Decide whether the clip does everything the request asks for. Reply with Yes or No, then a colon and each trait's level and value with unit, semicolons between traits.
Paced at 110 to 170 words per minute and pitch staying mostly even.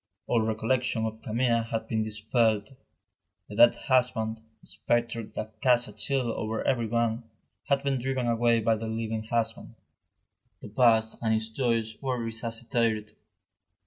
Yes: average, 145 wpm; narrow, 1.5 semitones